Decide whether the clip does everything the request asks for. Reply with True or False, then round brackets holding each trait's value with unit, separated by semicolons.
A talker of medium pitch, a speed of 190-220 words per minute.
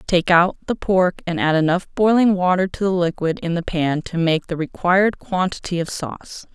True (175 Hz; 200 wpm)